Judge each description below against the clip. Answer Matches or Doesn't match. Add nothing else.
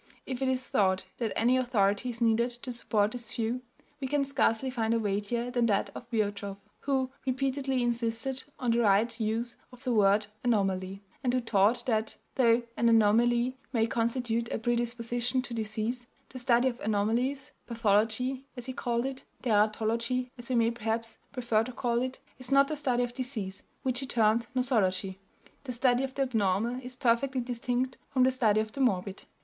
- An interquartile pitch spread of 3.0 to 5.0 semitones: Doesn't match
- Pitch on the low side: Doesn't match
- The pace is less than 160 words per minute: Doesn't match